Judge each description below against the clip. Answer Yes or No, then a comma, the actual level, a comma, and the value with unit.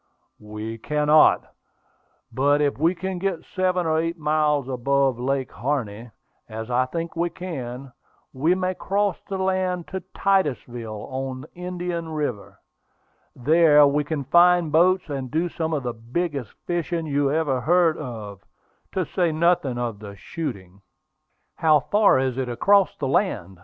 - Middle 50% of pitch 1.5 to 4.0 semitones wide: No, wide, 5.4 semitones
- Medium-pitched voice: Yes, medium, 150 Hz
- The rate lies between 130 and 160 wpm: Yes, average, 145 wpm